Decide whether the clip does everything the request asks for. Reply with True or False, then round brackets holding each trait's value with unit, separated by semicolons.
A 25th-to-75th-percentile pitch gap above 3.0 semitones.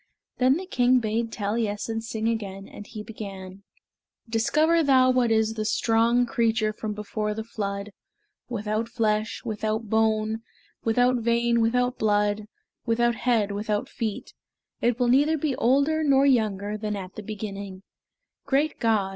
False (2.5 semitones)